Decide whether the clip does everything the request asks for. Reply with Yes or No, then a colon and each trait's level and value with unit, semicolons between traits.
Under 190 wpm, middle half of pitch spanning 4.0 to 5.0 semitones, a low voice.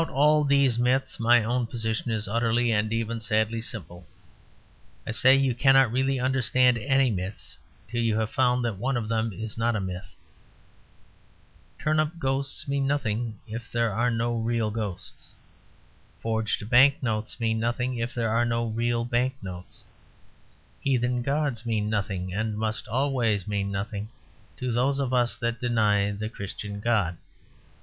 No: average, 155 wpm; average, 2.7 semitones; low, 115 Hz